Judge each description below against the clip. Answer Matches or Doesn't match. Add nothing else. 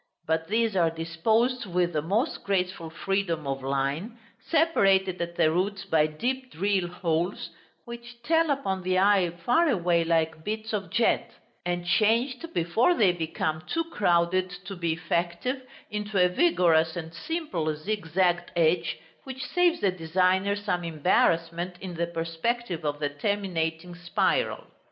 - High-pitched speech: Doesn't match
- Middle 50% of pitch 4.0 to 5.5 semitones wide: Matches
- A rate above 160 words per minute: Doesn't match